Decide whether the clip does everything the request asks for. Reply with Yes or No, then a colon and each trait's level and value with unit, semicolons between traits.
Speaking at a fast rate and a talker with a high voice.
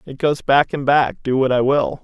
No: fast, 265 wpm; low, 135 Hz